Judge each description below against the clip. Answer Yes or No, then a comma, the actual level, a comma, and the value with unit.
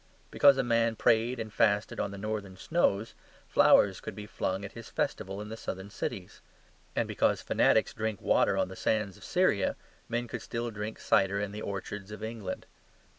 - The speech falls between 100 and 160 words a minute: No, average, 185 wpm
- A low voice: Yes, low, 105 Hz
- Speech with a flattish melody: Yes, narrow, 2.2 semitones